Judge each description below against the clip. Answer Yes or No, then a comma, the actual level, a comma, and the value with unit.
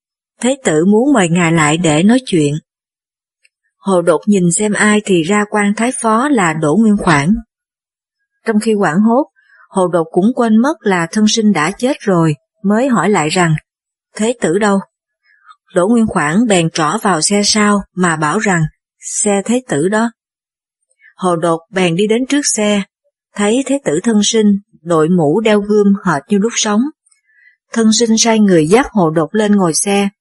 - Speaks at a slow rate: No, average, 180 wpm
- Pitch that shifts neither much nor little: Yes, average, 4.2 semitones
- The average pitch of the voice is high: Yes, high, 210 Hz